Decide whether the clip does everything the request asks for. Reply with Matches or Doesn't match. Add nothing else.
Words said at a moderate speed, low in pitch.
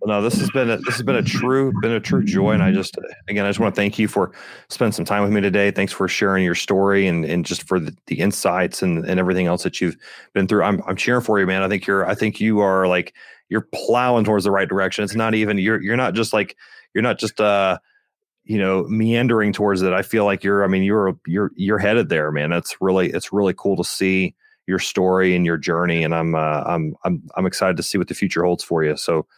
Doesn't match